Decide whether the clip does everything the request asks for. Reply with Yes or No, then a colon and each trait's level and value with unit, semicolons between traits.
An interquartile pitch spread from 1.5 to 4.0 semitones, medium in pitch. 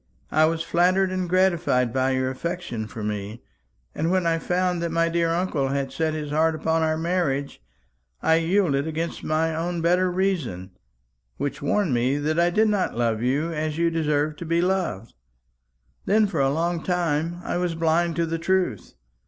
Yes: average, 3.5 semitones; medium, 165 Hz